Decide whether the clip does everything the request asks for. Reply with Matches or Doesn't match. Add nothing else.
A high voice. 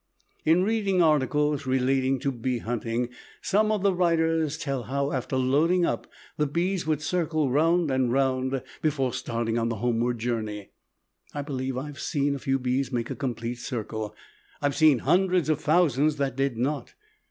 Doesn't match